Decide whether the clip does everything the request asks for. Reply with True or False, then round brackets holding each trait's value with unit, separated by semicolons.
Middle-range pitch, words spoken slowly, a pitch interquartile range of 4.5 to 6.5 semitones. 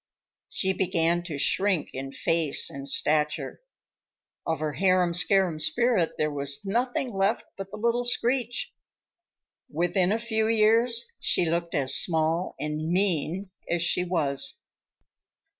True (180 Hz; 130 wpm; 5.3 semitones)